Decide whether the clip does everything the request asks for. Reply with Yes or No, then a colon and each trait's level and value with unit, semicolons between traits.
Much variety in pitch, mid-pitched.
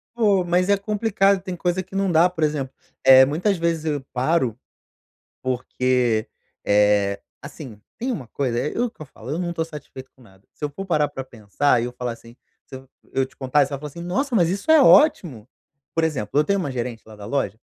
Yes: wide, 6.3 semitones; medium, 145 Hz